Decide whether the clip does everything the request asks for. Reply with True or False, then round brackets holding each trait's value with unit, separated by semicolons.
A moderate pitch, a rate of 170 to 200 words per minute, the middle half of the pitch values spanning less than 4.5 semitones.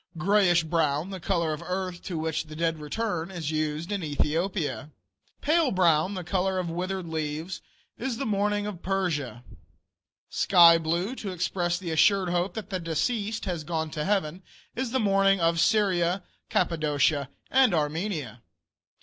False (175 Hz; 160 wpm; 3.6 semitones)